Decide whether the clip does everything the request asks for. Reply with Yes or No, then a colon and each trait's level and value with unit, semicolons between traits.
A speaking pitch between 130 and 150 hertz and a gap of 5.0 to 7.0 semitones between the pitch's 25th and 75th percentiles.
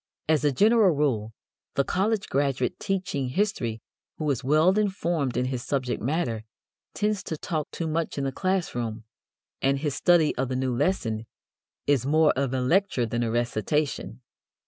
Yes: medium, 140 Hz; wide, 5.6 semitones